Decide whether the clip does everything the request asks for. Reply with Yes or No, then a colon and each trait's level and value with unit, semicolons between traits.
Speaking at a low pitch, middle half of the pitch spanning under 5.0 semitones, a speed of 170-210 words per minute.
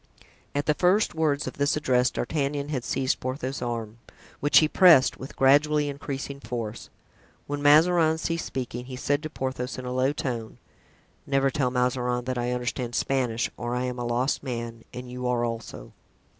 Yes: low, 130 Hz; average, 2.8 semitones; average, 175 wpm